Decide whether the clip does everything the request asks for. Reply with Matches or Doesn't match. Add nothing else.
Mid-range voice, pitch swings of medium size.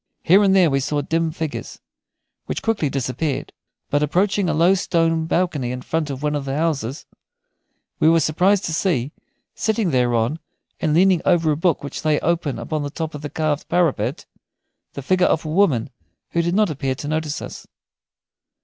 Matches